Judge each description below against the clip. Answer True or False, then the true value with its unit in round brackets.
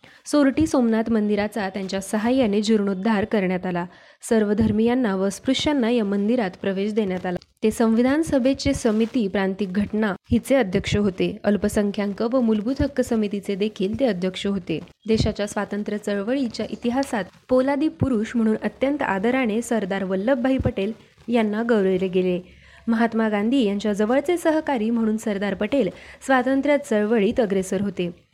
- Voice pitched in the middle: False (220 Hz)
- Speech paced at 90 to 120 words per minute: False (130 wpm)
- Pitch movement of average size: True (3.6 semitones)